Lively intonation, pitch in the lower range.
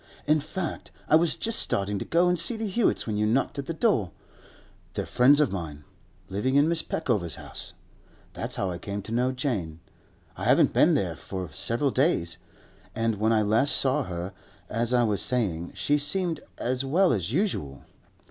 Yes: wide, 7.3 semitones; low, 125 Hz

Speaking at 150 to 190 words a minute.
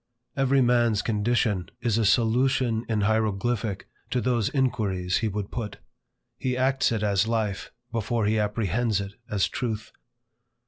No: average, 140 wpm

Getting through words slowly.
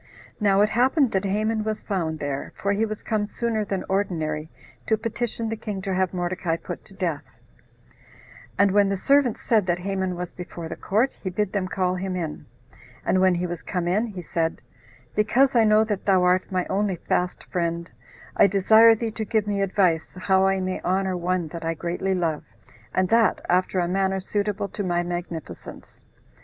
No: average, 195 wpm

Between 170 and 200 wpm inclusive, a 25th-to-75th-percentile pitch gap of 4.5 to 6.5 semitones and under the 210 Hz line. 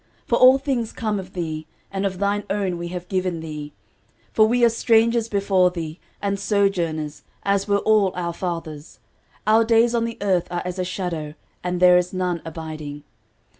No: average, 185 wpm; average, 3.5 semitones; medium, 185 Hz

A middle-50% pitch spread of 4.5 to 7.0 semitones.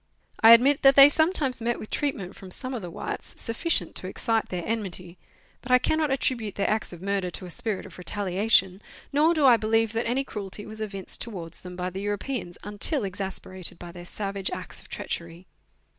Yes: average, 4.9 semitones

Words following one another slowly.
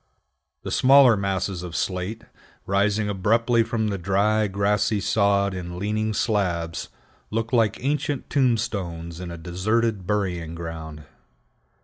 Yes: slow, 120 wpm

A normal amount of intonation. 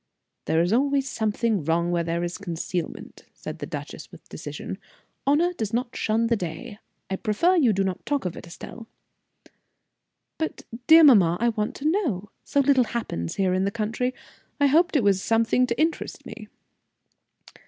No: wide, 6.9 semitones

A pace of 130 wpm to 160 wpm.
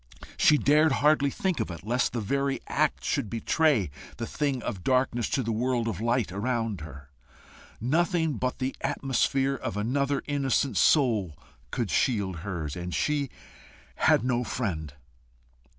Yes: average, 150 wpm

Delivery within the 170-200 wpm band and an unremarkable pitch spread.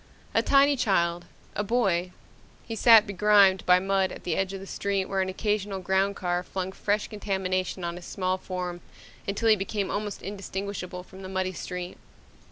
No: average, 175 wpm; narrow, 1.8 semitones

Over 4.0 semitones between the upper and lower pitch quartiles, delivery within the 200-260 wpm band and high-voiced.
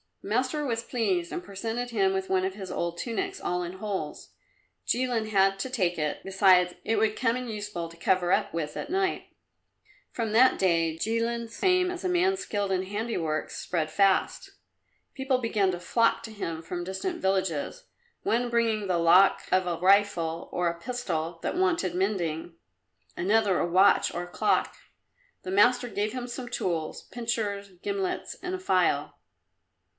No: average, 4.9 semitones; average, 170 wpm; high, 200 Hz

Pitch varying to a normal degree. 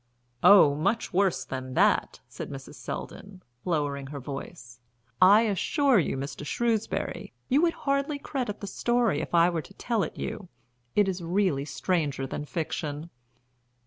No: wide, 6.7 semitones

